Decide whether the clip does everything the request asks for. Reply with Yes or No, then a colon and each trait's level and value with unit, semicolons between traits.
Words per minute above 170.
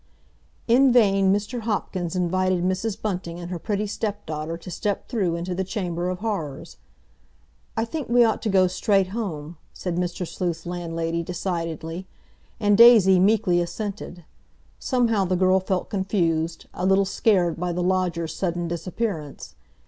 No: average, 150 wpm